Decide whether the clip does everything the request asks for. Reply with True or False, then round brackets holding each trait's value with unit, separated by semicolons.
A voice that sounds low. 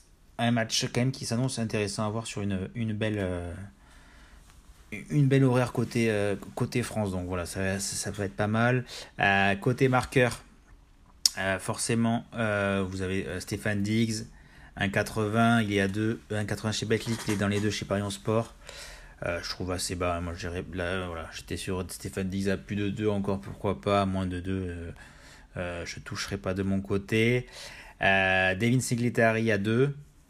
True (100 Hz)